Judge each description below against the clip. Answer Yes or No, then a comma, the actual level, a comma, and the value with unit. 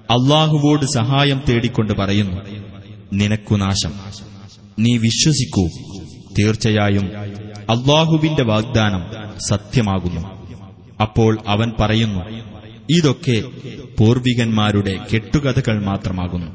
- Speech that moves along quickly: No, average, 70 wpm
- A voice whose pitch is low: Yes, low, 110 Hz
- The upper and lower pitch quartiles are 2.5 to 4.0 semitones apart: Yes, average, 3.1 semitones